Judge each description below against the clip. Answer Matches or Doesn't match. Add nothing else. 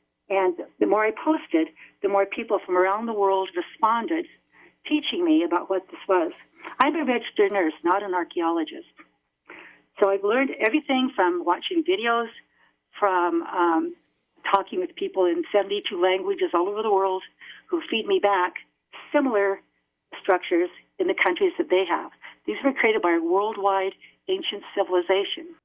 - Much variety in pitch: Matches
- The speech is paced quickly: Doesn't match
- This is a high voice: Matches